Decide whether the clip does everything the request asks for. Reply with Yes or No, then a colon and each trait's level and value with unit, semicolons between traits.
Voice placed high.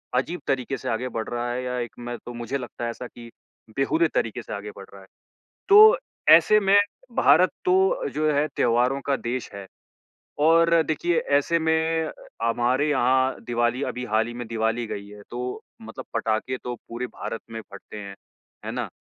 No: low, 125 Hz